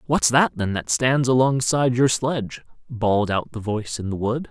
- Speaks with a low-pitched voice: Yes, low, 120 Hz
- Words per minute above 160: Yes, average, 200 wpm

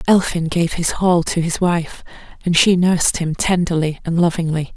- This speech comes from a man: No, female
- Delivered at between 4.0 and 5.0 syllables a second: Yes, 4.8 syllables/s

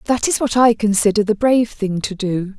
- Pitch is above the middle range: Yes, high, 215 Hz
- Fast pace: Yes, fast, 230 wpm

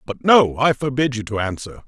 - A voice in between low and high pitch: No, low, 125 Hz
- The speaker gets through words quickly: Yes, fast, 225 wpm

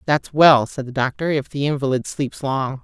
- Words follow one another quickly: Yes, fast, 210 wpm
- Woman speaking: Yes, female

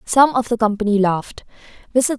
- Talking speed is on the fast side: No, slow, 135 wpm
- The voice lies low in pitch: No, high, 225 Hz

